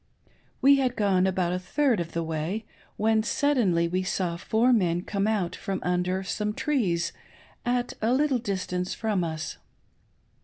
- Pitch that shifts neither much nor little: Yes, average, 4.2 semitones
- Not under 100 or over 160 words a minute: Yes, average, 155 wpm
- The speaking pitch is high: Yes, high, 195 Hz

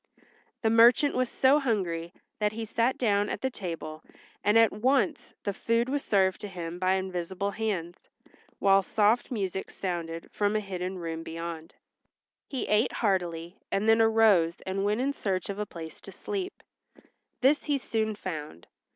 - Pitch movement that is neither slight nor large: Yes, average, 4.3 semitones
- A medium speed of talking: Yes, average, 165 wpm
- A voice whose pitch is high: Yes, high, 200 Hz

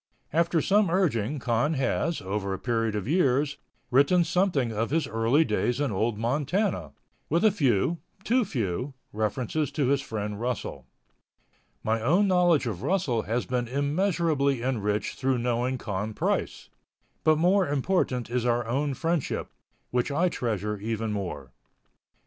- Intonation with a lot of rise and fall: Yes, wide, 6.2 semitones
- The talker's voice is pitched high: No, low, 130 Hz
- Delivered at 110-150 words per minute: Yes, average, 145 wpm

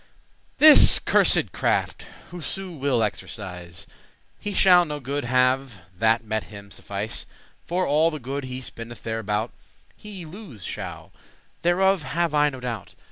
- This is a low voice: Yes, low, 130 Hz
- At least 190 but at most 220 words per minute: No, slow, 135 wpm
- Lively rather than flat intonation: Yes, wide, 7.2 semitones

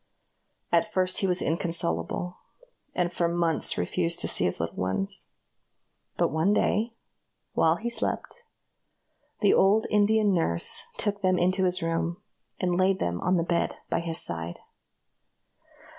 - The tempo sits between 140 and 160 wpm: Yes, average, 145 wpm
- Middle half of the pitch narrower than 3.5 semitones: Yes, average, 2.9 semitones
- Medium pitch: Yes, medium, 175 Hz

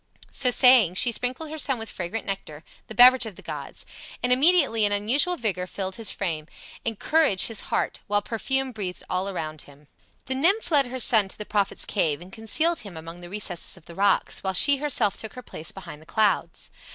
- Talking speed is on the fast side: Yes, fast, 210 wpm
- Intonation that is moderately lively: No, wide, 5.7 semitones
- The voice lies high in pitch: Yes, high, 215 Hz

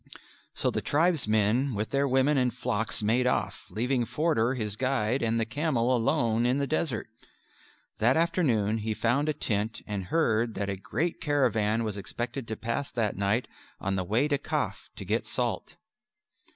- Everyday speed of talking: Yes, average, 170 wpm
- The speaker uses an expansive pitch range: No, average, 4.1 semitones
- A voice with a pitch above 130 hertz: No, low, 120 Hz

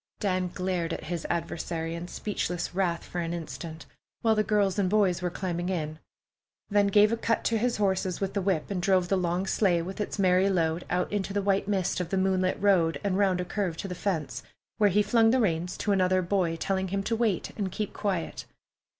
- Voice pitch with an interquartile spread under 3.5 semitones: Yes, narrow, 2.5 semitones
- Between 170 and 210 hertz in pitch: Yes, medium, 185 Hz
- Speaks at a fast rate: Yes, fast, 220 wpm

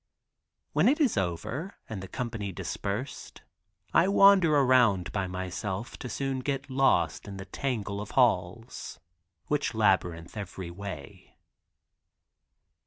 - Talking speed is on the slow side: Yes, slow, 120 wpm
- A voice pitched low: Yes, low, 105 Hz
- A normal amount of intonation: No, wide, 6.3 semitones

